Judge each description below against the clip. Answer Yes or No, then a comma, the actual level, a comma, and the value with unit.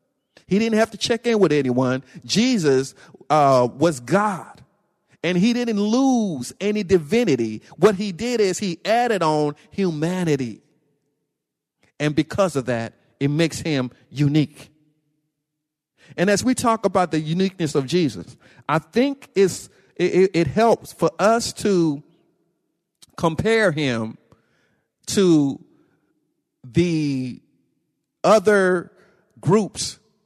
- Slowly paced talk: Yes, slow, 115 wpm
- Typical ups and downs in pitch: No, wide, 5.9 semitones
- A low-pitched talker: No, medium, 165 Hz